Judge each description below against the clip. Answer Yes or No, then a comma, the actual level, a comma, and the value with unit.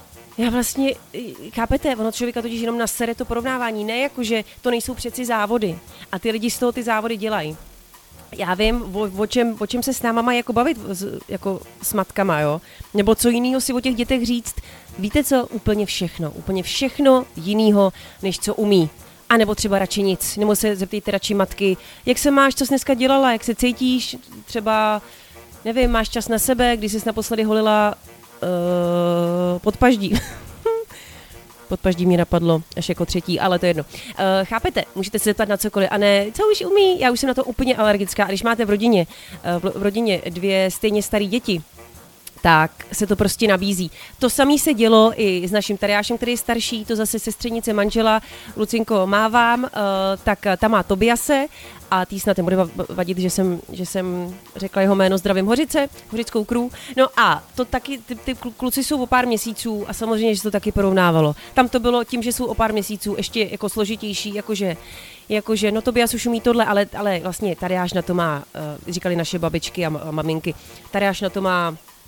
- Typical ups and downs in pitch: Yes, average, 3.8 semitones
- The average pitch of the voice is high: Yes, high, 215 Hz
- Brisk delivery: Yes, fast, 190 wpm